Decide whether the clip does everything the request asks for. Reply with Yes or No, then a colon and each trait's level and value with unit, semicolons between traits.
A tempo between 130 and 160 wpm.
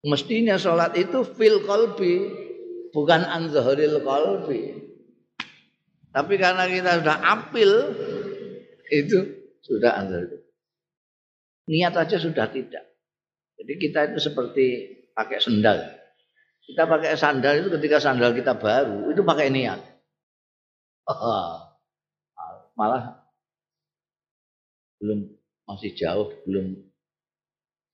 No: average, 90 wpm